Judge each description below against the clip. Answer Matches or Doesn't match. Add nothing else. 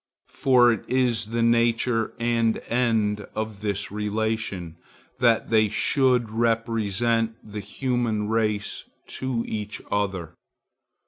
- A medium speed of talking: Doesn't match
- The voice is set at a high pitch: Doesn't match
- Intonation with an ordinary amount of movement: Doesn't match